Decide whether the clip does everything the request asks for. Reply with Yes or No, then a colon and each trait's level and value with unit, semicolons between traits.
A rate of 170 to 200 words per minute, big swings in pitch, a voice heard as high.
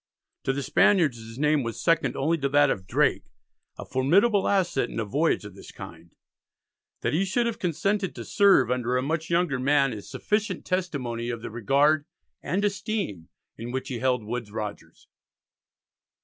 No: average, 175 wpm; wide, 7.0 semitones; medium, 140 Hz